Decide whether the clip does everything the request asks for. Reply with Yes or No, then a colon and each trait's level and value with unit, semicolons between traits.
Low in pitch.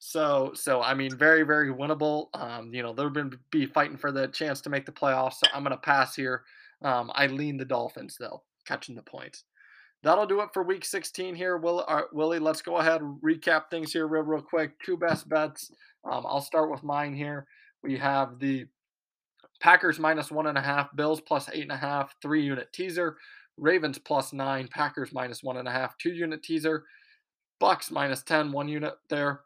No: medium, 150 Hz